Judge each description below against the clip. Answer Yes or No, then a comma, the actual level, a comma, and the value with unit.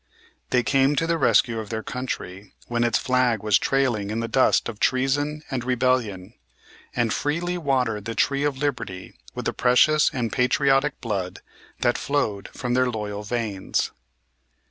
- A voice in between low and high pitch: No, low, 125 Hz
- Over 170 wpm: No, average, 160 wpm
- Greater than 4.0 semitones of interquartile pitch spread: No, average, 3.7 semitones